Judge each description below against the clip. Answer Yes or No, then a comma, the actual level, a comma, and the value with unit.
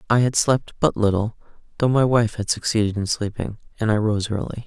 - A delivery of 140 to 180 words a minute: No, fast, 205 wpm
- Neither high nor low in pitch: No, low, 110 Hz